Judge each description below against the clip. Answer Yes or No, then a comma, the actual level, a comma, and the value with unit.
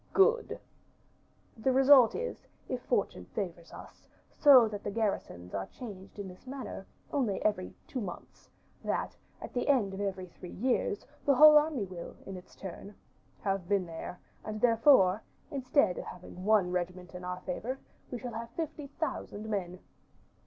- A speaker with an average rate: Yes, average, 160 wpm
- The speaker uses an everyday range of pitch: No, wide, 6.0 semitones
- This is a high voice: Yes, high, 210 Hz